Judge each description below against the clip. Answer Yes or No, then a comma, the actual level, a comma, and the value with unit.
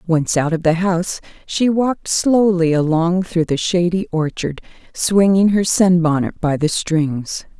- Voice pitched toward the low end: No, medium, 175 Hz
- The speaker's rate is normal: Yes, average, 150 wpm